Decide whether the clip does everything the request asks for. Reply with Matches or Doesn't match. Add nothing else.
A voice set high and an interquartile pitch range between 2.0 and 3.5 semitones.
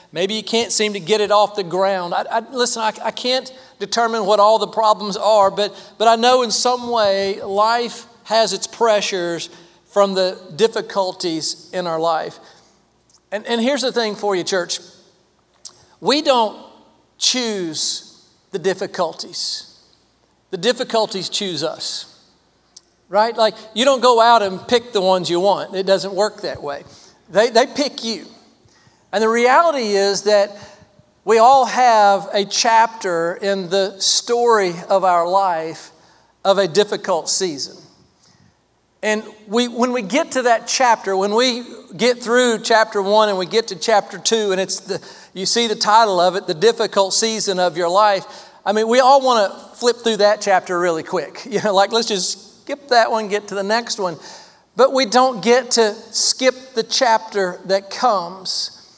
Matches